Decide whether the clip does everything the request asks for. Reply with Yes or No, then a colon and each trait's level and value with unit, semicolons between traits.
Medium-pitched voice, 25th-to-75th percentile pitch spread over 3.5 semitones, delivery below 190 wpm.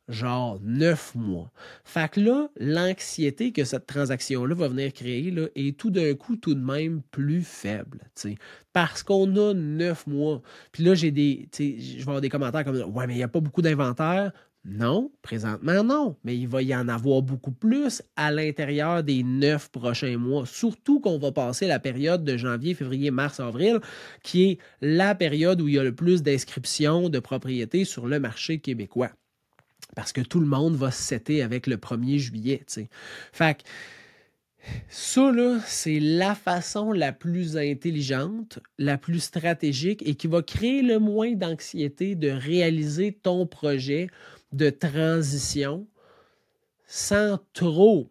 Yes: medium, 150 Hz; average, 5.1 semitones; average, 165 wpm